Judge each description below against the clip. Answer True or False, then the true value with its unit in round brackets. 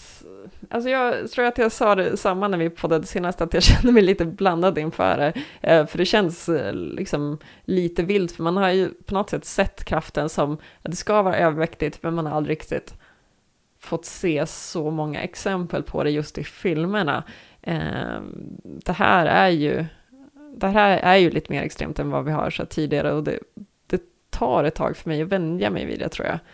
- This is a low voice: False (175 Hz)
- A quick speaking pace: True (200 wpm)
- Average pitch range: True (3.8 semitones)